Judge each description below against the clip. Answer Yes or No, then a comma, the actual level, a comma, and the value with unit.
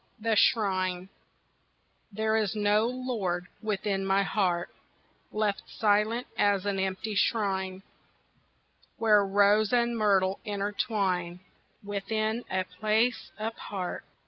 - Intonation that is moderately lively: No, narrow, 2.2 semitones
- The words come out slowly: Yes, slow, 100 wpm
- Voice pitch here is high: Yes, high, 205 Hz